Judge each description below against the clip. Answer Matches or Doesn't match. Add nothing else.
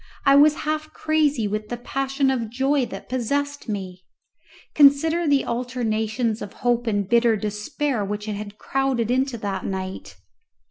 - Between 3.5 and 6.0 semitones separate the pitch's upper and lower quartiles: Matches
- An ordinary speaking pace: Matches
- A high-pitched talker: Matches